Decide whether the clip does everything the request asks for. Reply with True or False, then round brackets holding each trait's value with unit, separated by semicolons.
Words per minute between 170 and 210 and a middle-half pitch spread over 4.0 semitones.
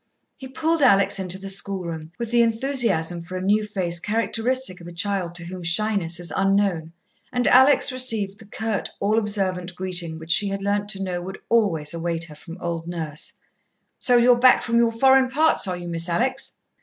True (195 wpm; 5.0 semitones)